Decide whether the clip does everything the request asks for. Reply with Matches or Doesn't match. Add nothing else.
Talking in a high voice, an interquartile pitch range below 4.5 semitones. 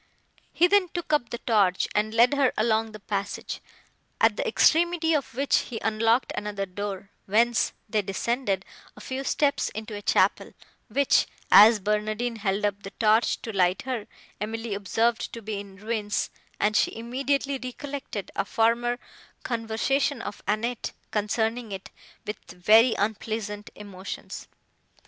Matches